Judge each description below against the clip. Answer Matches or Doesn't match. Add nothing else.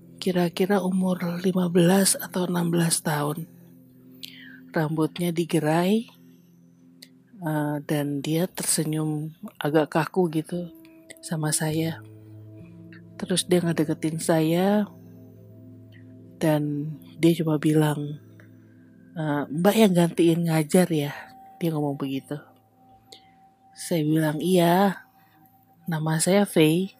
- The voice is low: Doesn't match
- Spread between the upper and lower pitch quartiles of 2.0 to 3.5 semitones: Doesn't match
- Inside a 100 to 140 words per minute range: Doesn't match